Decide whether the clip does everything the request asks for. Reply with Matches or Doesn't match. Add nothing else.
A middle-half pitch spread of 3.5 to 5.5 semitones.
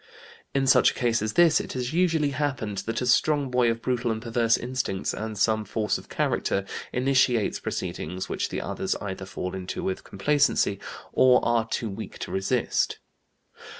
Matches